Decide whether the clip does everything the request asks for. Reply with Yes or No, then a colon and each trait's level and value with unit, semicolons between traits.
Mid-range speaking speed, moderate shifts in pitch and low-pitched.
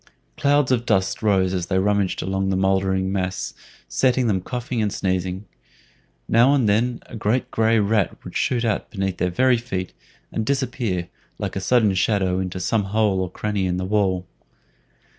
Yes: average, 175 wpm; average, 3.5 semitones; low, 100 Hz